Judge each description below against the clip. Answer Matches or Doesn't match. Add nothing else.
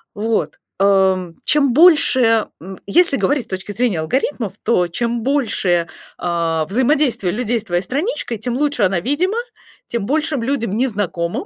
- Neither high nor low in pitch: Doesn't match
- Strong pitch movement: Matches